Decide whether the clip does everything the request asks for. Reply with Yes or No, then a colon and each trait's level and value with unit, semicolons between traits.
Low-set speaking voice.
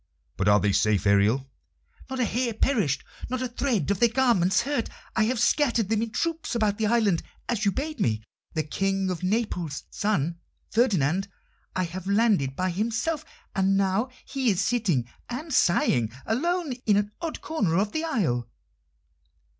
No: high, 205 Hz